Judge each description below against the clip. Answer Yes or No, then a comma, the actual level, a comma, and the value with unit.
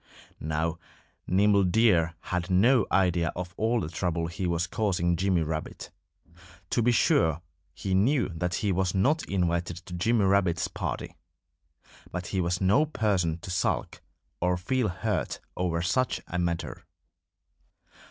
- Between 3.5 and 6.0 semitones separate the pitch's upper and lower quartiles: No, average, 2.8 semitones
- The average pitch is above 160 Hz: No, very low, 90 Hz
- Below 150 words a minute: Yes, average, 140 wpm